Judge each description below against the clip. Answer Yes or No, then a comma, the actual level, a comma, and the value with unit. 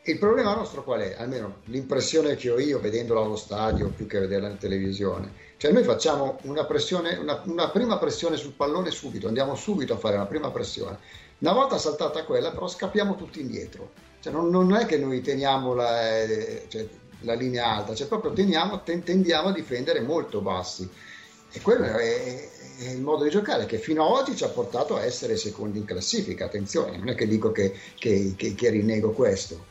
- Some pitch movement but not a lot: No, wide, 8.1 semitones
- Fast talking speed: Yes, fast, 195 wpm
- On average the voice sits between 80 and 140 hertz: Yes, low, 135 Hz